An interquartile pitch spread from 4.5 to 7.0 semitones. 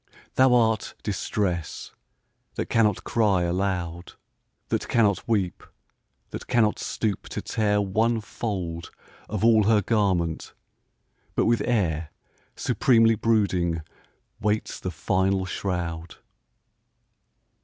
No: average, 4.0 semitones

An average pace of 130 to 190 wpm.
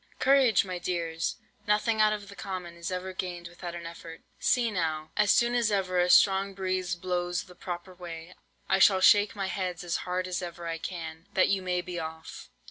No: fast, 205 wpm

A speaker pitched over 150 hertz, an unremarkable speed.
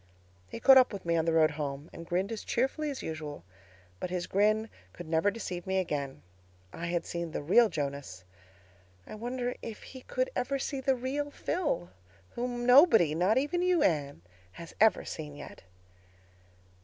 Yes: high, 190 Hz; average, 170 wpm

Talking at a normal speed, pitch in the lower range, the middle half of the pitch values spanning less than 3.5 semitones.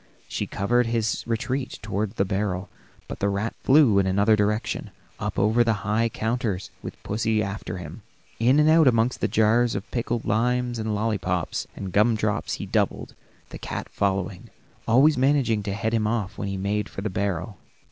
Yes: average, 180 wpm; low, 110 Hz; average, 2.9 semitones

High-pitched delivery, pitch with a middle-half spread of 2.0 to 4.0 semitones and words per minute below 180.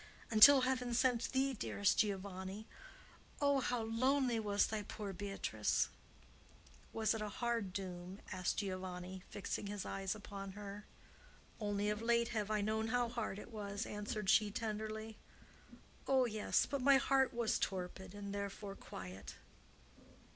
Yes: high, 210 Hz; average, 2.9 semitones; average, 140 wpm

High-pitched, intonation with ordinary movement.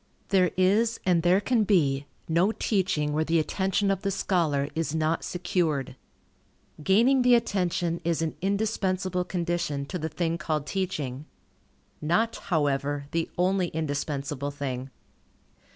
No: medium, 170 Hz; average, 4.3 semitones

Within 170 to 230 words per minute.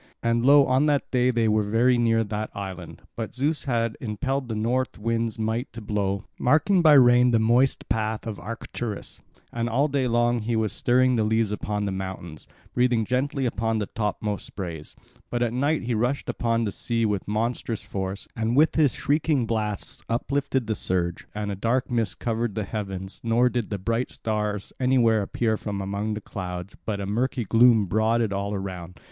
Yes: average, 190 wpm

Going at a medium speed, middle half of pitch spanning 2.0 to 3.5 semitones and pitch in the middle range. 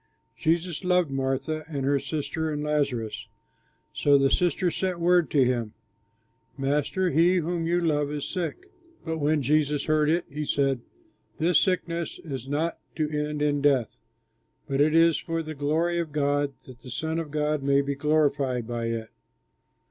Yes: average, 165 wpm; average, 2.9 semitones; medium, 150 Hz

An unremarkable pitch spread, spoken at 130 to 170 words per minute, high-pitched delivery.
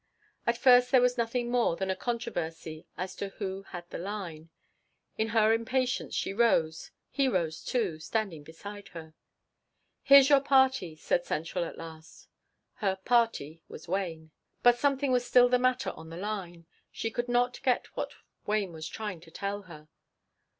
No: wide, 6.6 semitones; average, 165 wpm; high, 205 Hz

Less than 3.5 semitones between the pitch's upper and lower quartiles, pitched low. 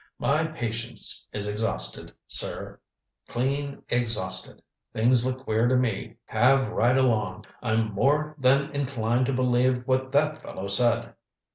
Yes: average, 3.0 semitones; low, 125 Hz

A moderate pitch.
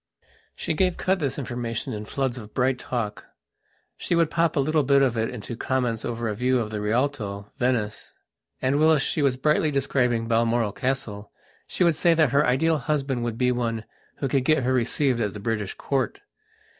No: low, 125 Hz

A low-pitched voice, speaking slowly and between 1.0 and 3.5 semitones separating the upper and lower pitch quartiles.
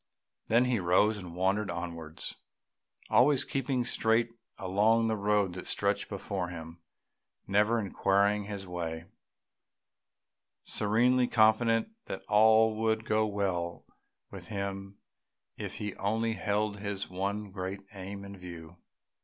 Yes: low, 100 Hz; slow, 120 wpm; average, 2.9 semitones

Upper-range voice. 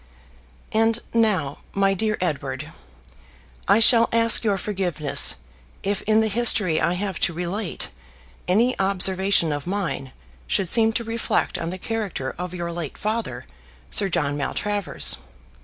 Yes: high, 195 Hz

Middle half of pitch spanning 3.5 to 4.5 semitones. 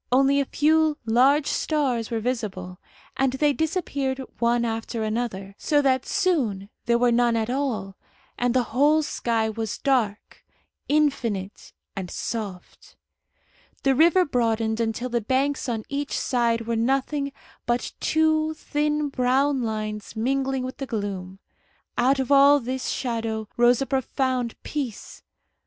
Yes: average, 3.8 semitones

